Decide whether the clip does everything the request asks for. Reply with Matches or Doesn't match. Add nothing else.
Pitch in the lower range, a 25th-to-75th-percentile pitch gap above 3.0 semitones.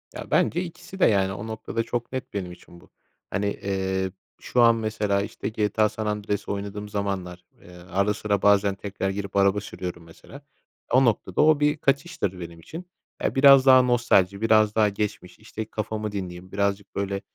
Doesn't match